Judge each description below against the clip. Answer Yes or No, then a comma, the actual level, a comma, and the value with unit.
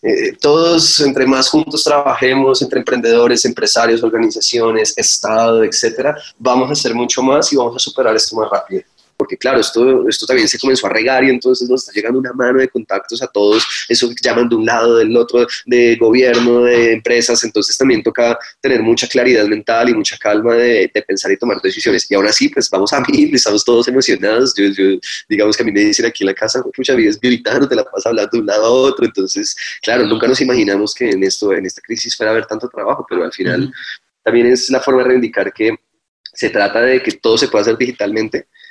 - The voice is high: No, low, 130 Hz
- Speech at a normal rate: No, fast, 220 wpm